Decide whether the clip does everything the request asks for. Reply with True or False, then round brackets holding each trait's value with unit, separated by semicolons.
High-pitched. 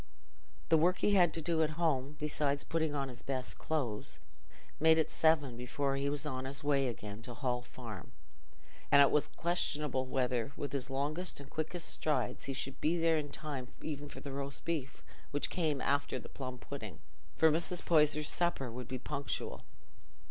False (145 Hz)